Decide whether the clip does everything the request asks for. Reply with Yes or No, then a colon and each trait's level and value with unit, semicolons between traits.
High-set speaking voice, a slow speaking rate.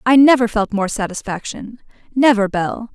Yes: high, 225 Hz; slow, 120 wpm